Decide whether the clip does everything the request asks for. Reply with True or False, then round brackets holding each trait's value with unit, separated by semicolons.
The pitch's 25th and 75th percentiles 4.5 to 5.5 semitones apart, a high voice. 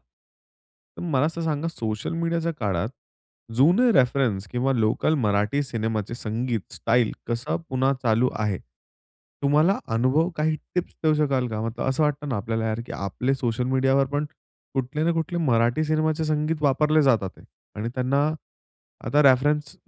False (5.0 semitones; 135 Hz)